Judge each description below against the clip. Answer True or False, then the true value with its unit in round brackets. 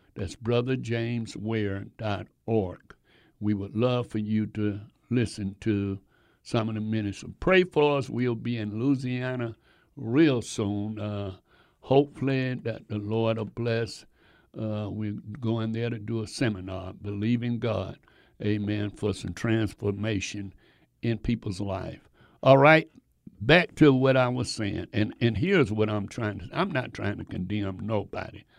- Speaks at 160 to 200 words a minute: False (145 wpm)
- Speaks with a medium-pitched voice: False (110 Hz)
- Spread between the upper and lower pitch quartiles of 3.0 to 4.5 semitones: False (2.6 semitones)